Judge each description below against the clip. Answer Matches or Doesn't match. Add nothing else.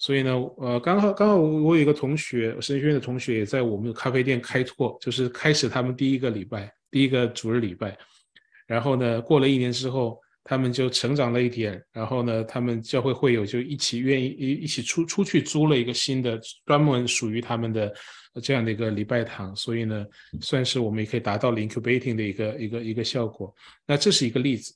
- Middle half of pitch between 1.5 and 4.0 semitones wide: Matches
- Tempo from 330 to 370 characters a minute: Matches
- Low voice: Matches